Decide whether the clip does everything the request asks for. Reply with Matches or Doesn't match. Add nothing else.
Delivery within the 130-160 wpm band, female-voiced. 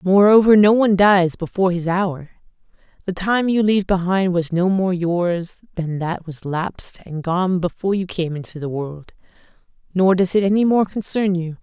Doesn't match